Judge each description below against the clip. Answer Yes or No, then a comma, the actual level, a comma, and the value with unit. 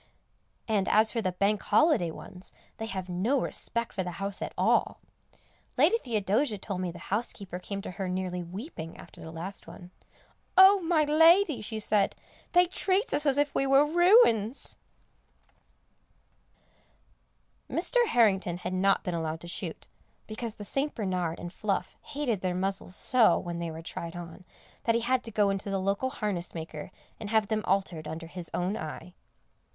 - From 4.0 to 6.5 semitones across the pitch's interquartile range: Yes, average, 5.2 semitones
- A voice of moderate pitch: No, high, 200 Hz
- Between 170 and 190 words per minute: Yes, average, 175 wpm